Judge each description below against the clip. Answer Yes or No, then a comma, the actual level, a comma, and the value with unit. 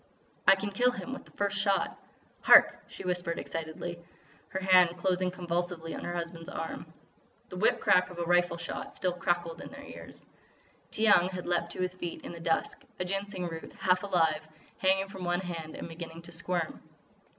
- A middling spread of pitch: No, narrow, 1.9 semitones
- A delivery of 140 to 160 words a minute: No, average, 185 wpm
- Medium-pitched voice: Yes, medium, 180 Hz